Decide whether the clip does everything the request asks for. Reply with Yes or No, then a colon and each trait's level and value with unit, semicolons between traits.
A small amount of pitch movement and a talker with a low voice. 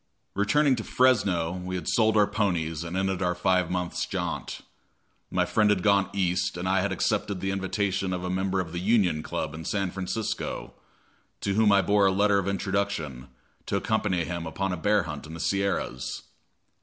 Yes: narrow, 2.3 semitones; very low, 95 Hz